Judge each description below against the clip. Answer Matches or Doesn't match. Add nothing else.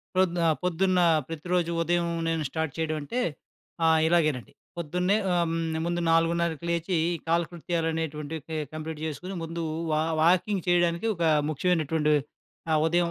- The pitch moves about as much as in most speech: Doesn't match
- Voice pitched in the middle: Matches